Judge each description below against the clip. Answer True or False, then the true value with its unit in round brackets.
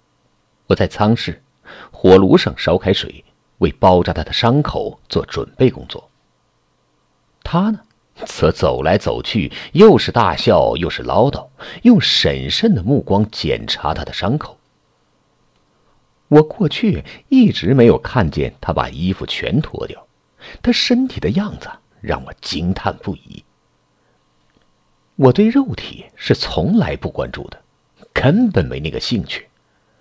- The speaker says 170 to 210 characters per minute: True (190 characters per minute)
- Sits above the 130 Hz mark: False (115 Hz)